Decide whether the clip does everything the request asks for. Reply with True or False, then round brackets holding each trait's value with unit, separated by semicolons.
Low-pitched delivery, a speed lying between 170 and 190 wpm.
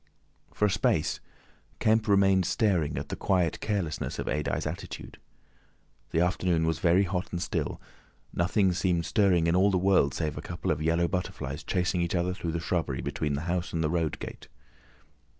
True (90 Hz; 180 wpm)